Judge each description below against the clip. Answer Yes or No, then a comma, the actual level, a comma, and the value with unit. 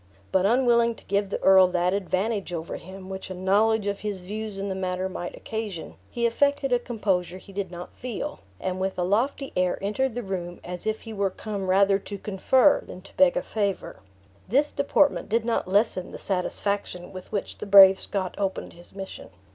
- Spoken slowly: No, average, 200 wpm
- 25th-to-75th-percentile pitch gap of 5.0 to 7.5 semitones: No, average, 3.0 semitones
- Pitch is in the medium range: No, high, 200 Hz